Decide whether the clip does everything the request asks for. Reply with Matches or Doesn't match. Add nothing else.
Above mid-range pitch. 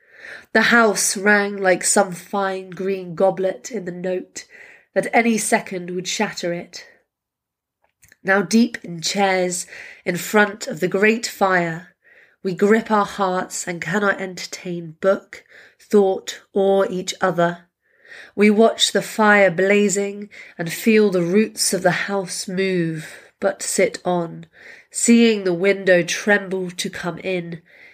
Matches